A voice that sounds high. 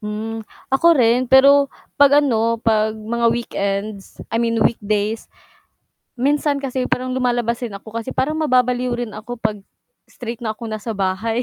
Yes: high, 235 Hz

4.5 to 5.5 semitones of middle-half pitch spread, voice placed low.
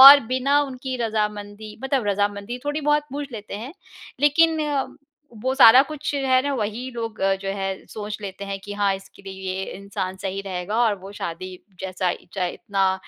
No: average, 5.1 semitones; high, 210 Hz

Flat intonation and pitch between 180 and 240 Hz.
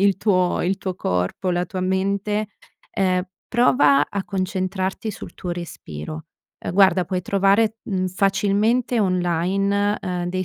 Yes: narrow, 1.9 semitones; high, 190 Hz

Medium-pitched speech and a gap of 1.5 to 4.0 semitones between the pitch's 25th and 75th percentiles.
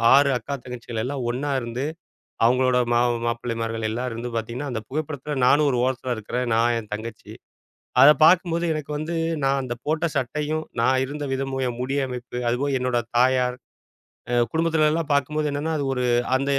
No: low, 130 Hz; average, 3.3 semitones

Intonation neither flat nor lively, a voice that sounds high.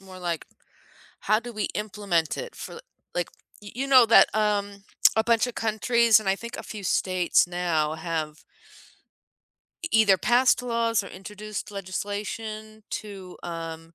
Yes: average, 3.8 semitones; high, 205 Hz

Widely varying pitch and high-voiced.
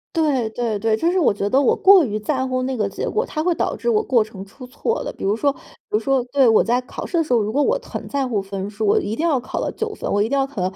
Yes: wide, 5.9 semitones; very high, 255 Hz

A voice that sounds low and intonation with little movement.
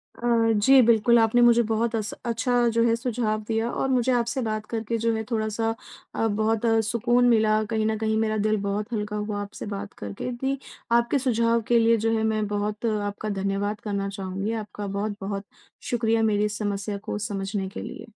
No: high, 220 Hz; narrow, 2.0 semitones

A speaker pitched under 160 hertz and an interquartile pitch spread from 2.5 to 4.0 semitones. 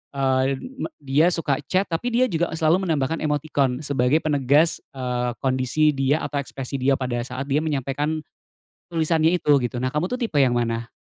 Yes: medium, 140 Hz; average, 3.4 semitones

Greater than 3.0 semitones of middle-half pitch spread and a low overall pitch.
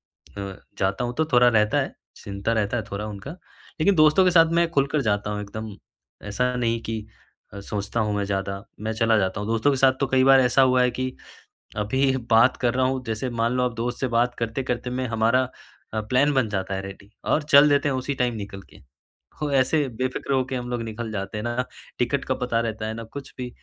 Yes: average, 3.5 semitones; low, 120 Hz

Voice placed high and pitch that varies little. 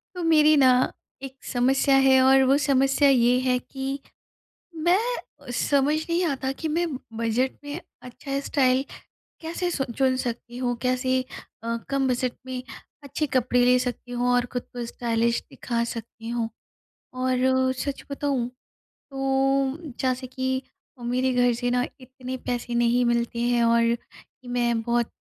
Yes: very high, 255 Hz; narrow, 1.9 semitones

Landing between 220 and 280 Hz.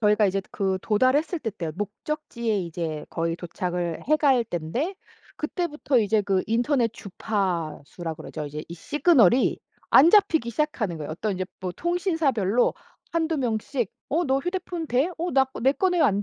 Yes: high, 230 Hz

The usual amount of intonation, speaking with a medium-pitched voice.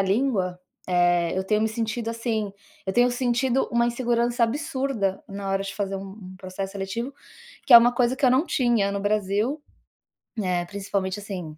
No: average, 3.9 semitones; high, 210 Hz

